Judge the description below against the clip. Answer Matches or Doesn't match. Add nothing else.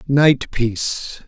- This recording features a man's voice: Matches